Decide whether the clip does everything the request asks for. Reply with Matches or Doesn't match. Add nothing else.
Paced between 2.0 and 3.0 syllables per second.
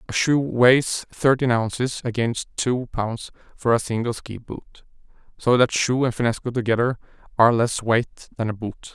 Doesn't match